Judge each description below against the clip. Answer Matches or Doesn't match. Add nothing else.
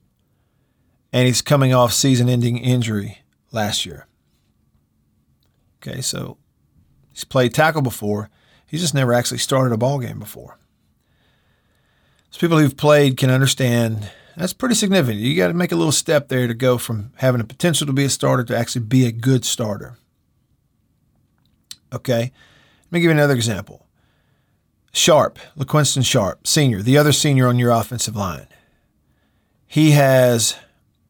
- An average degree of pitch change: Matches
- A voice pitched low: Matches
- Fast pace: Doesn't match